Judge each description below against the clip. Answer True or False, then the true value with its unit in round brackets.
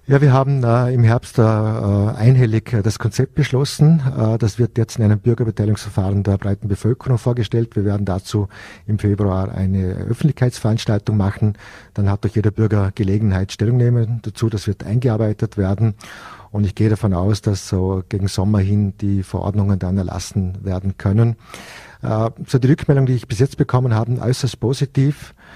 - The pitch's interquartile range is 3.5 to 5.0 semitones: False (3.1 semitones)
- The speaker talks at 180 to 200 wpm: False (170 wpm)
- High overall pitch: False (110 Hz)